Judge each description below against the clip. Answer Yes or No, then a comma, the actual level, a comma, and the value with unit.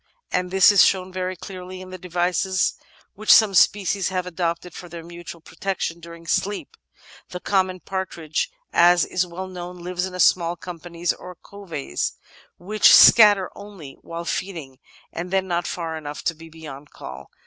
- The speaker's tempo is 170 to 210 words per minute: No, average, 160 wpm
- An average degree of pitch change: No, narrow, 1.9 semitones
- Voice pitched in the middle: Yes, medium, 180 Hz